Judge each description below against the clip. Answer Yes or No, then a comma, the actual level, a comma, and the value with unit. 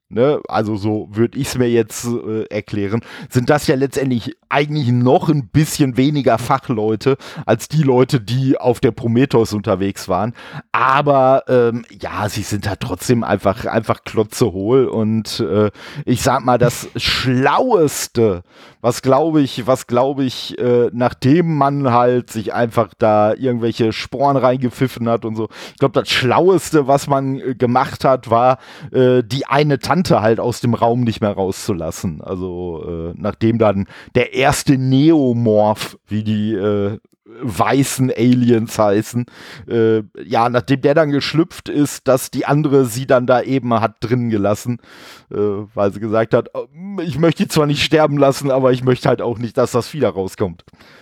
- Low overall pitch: Yes, low, 120 Hz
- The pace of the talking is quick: No, average, 160 wpm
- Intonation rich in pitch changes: No, average, 3.7 semitones